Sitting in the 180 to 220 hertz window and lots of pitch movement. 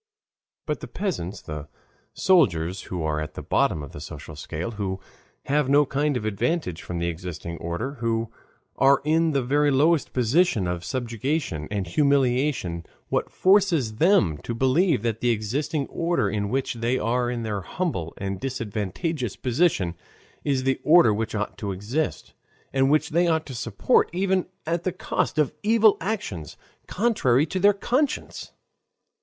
No: low, 125 Hz; wide, 7.9 semitones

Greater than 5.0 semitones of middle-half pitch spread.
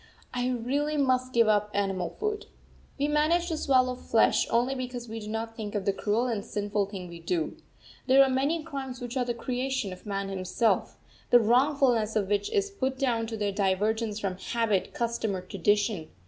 No: average, 4.3 semitones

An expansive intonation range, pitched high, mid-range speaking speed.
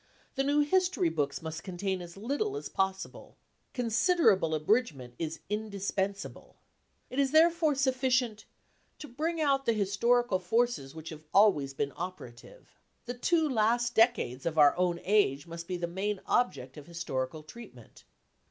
Yes: wide, 7.6 semitones; high, 200 Hz; average, 150 wpm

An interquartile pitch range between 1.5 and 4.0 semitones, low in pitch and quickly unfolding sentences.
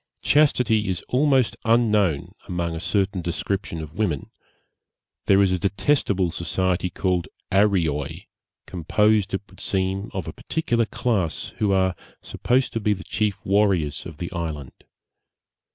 No: average, 3.6 semitones; very low, 95 Hz; slow, 135 wpm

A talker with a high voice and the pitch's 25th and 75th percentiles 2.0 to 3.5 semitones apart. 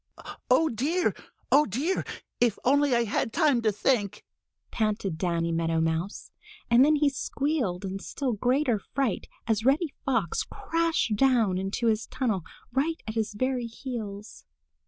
No: high, 235 Hz; average, 5.2 semitones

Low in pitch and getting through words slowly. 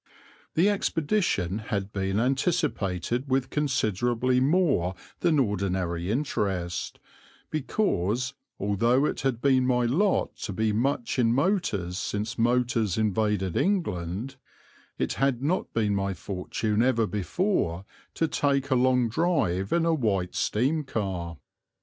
Yes: low, 115 Hz; slow, 125 wpm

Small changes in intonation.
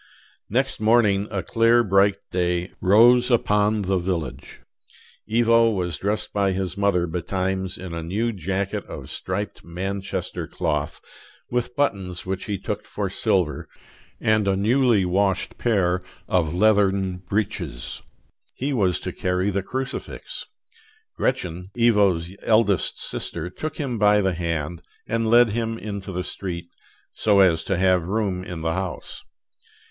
No: average, 3.2 semitones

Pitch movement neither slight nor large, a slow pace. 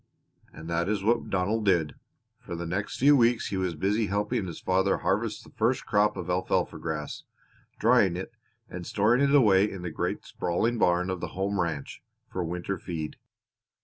No: average, 3.5 semitones; average, 180 wpm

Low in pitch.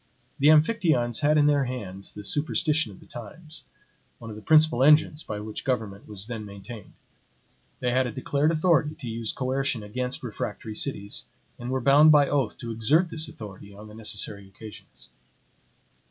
Yes: low, 125 Hz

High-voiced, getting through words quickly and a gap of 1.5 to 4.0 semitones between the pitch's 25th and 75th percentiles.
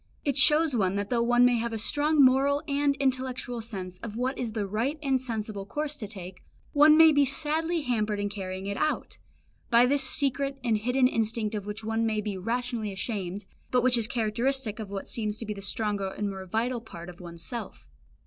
No: high, 230 Hz; fast, 210 wpm; average, 4.4 semitones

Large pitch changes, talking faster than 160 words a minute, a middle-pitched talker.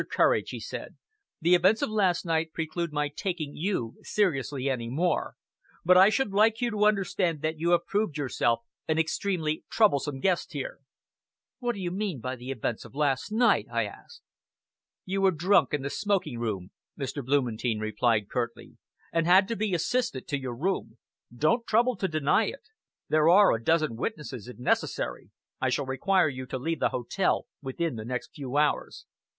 Yes: wide, 6.7 semitones; average, 180 wpm; medium, 155 Hz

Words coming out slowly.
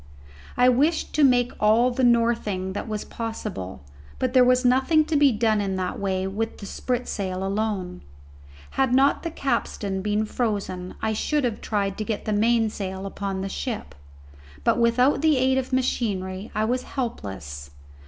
No: average, 165 wpm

